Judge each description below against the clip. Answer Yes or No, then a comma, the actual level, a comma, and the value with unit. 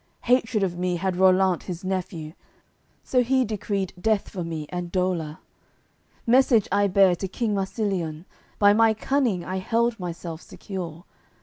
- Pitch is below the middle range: No, high, 190 Hz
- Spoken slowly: No, average, 145 wpm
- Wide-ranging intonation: No, average, 3.6 semitones